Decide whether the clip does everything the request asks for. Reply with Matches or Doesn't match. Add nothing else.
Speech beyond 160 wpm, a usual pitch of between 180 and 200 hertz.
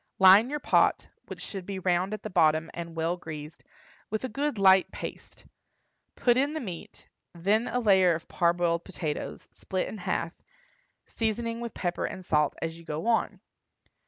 Matches